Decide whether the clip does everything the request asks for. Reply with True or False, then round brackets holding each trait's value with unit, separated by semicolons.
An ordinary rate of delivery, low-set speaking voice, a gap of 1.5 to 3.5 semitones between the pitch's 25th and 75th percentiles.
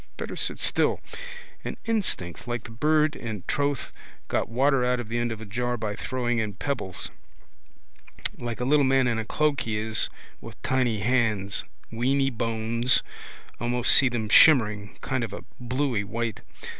True (165 wpm; 120 Hz; 2.9 semitones)